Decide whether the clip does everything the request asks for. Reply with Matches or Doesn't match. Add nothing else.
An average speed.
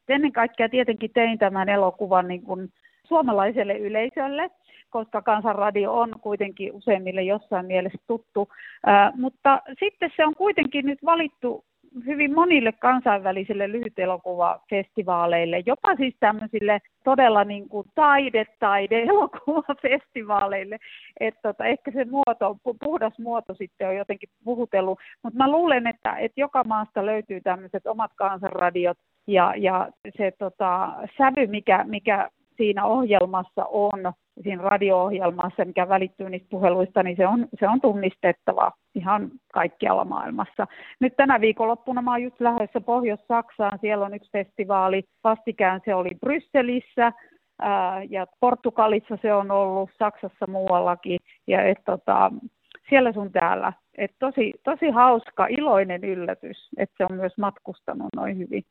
Matches